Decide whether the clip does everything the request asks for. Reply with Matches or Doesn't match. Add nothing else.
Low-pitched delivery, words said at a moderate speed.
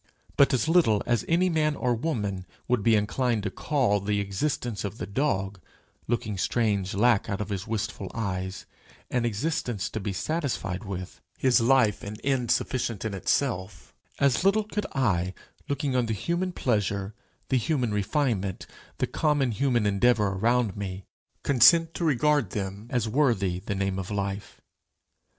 Matches